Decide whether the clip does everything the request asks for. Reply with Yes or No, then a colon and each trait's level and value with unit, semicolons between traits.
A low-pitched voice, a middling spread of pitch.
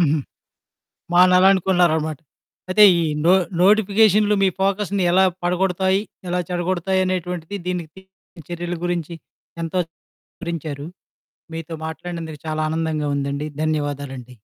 No: medium, 175 Hz; average, 3.1 semitones